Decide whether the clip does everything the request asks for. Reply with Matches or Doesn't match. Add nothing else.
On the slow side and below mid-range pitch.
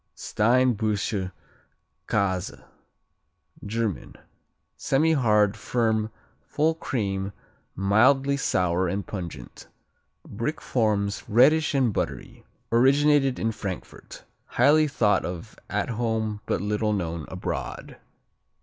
Matches